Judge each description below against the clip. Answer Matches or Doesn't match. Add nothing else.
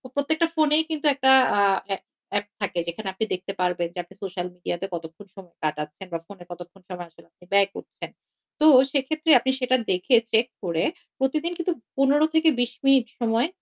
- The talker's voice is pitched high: Matches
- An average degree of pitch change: Doesn't match